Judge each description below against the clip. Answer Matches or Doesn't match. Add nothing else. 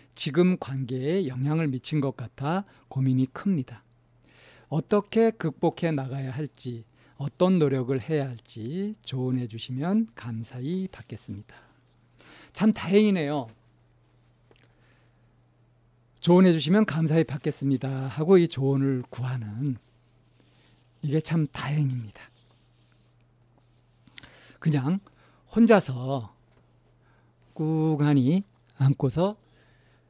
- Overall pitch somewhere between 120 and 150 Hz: Matches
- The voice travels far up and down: Doesn't match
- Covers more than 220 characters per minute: Doesn't match